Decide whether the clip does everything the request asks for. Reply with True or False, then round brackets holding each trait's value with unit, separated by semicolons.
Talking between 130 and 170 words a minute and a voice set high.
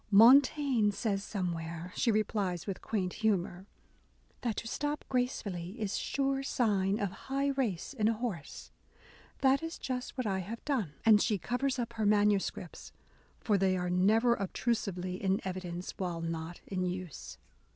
True (160 wpm; 205 Hz)